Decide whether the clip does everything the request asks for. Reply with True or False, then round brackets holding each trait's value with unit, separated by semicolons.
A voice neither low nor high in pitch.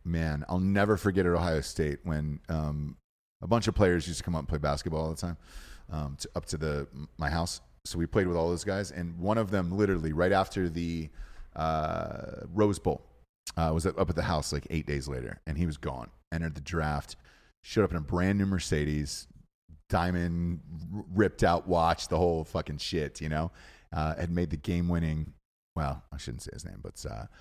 False (85 Hz)